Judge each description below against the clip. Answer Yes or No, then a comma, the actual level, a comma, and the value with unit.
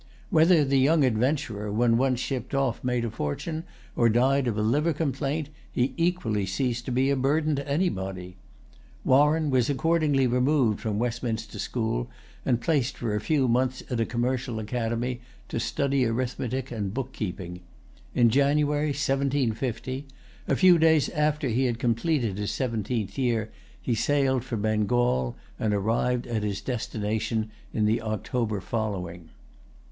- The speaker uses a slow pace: No, average, 150 wpm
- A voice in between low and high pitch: No, low, 125 Hz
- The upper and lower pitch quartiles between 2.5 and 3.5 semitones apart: No, average, 4.0 semitones